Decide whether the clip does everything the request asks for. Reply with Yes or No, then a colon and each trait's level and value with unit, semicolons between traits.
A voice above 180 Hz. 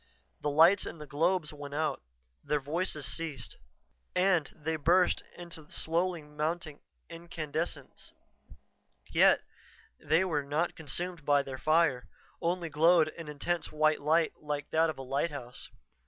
No: medium, 155 Hz